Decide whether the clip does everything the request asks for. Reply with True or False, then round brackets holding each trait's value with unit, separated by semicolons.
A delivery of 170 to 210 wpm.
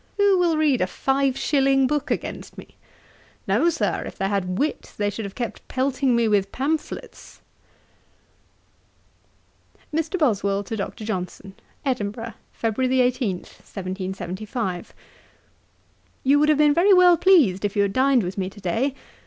False (145 wpm)